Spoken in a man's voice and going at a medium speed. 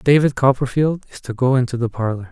No: male; fast, 210 wpm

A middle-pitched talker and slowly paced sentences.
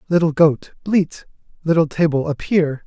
Yes: medium, 160 Hz; slow, 125 wpm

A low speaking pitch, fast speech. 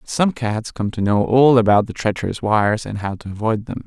Yes: low, 110 Hz; fast, 250 wpm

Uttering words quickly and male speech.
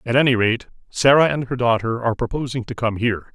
Yes: fast, 215 wpm; male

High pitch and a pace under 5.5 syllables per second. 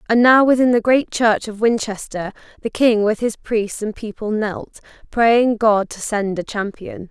Yes: high, 220 Hz; 4.3 syllables/s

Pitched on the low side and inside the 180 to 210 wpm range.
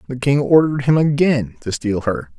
Yes: low, 130 Hz; average, 200 wpm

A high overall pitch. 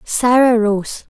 Yes: high, 230 Hz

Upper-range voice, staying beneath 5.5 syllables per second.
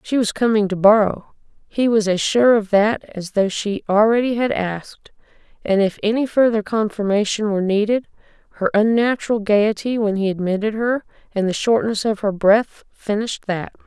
Yes: high, 215 Hz; 5.1 syllables/s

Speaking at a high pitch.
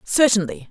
Yes: high, 215 Hz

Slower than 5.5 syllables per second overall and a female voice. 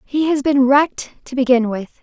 Yes: 5.0 syllables/s; female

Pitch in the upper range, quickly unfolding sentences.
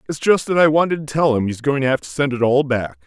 No: low, 135 Hz; fast, 335 wpm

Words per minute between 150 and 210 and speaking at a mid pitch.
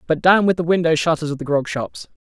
No: fast, 270 wpm; medium, 160 Hz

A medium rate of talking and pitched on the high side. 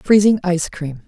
No: average, 165 wpm; medium, 180 Hz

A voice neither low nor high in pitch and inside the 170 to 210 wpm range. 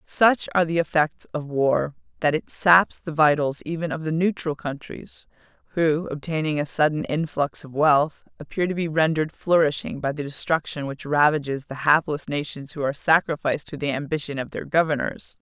Yes: medium, 155 Hz; average, 175 wpm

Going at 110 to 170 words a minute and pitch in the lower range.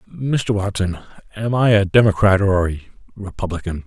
Yes: average, 140 wpm; low, 100 Hz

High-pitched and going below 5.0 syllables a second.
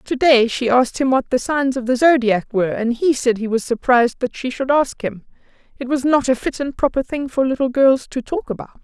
No: very high, 255 Hz; 5.6 syllables/s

